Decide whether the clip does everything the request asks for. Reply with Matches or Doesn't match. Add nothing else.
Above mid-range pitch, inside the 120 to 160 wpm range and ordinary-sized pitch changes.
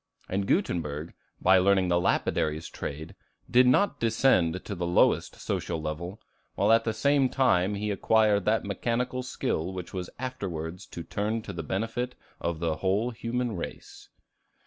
Doesn't match